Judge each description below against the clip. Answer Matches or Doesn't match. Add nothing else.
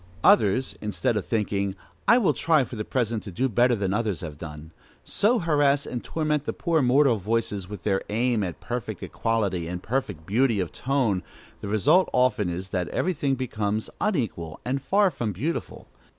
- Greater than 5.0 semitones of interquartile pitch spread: Matches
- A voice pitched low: Matches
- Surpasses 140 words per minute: Matches